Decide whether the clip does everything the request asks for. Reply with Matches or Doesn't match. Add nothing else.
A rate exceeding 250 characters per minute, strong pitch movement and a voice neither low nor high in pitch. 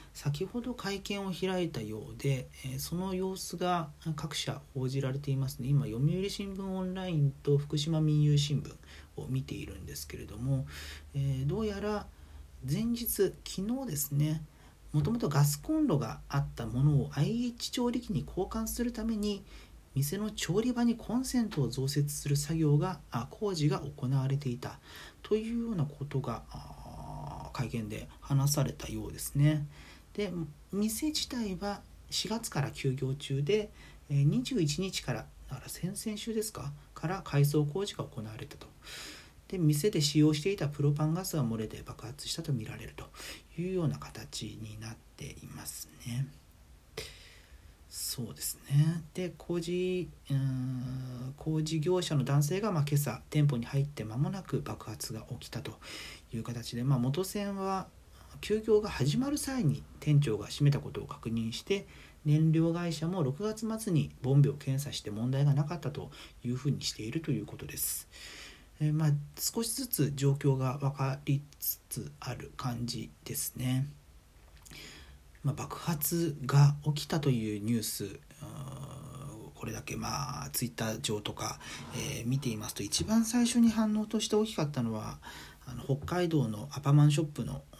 Matches